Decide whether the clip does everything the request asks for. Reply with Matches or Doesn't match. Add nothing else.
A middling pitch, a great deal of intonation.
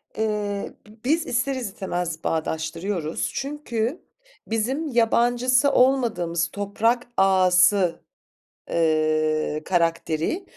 Doesn't match